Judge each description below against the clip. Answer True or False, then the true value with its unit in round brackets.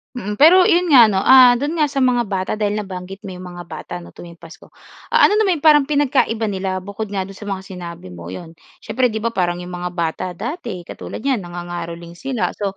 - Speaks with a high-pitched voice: True (200 Hz)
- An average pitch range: False (6.3 semitones)